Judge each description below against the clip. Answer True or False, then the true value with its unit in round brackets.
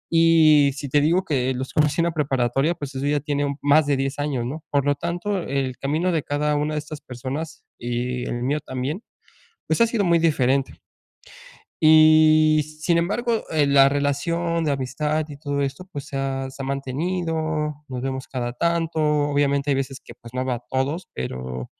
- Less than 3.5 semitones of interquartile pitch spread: True (2.8 semitones)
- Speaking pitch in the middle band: True (145 Hz)